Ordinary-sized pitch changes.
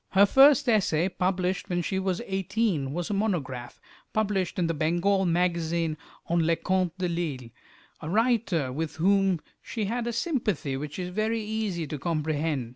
Yes: average, 4.0 semitones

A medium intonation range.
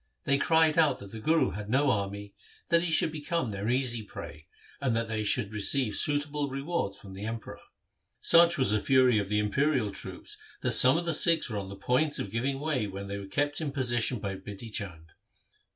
No: wide, 6.1 semitones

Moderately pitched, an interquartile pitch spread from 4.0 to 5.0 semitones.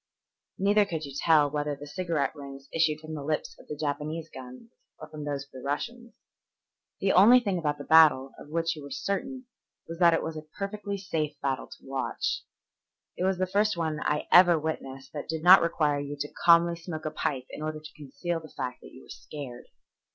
No: medium, 155 Hz; average, 3.2 semitones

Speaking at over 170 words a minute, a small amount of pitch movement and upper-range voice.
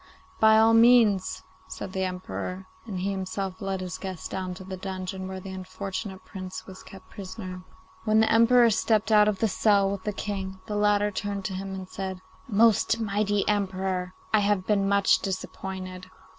Yes: average, 180 wpm; narrow, 1.9 semitones; high, 195 Hz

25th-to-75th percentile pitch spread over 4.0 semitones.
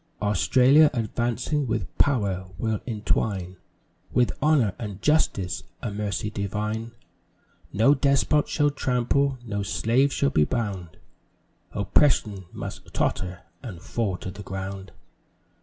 Yes: average, 4.9 semitones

